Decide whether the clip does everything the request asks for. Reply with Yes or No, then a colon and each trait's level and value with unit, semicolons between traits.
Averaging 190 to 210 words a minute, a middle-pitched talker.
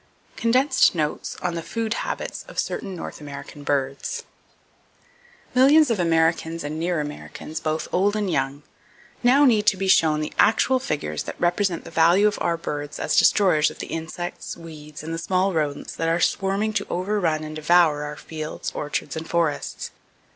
No: average, 170 wpm; medium, 165 Hz